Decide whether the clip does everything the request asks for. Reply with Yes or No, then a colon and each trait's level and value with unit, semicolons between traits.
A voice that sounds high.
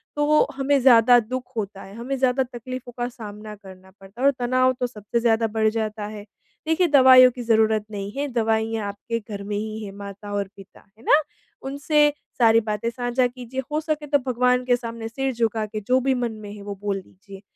Yes: high, 230 Hz